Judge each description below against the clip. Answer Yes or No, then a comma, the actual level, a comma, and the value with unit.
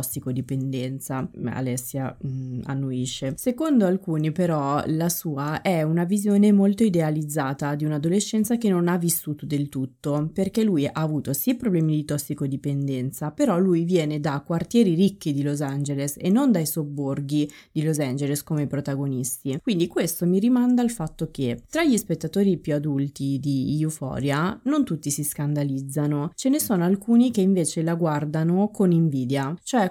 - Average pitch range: Yes, average, 4.7 semitones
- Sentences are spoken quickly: No, average, 155 wpm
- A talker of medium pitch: Yes, medium, 155 Hz